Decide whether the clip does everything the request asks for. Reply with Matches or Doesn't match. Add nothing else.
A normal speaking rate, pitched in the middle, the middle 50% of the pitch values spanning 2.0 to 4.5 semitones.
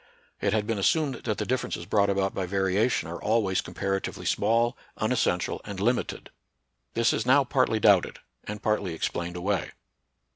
Doesn't match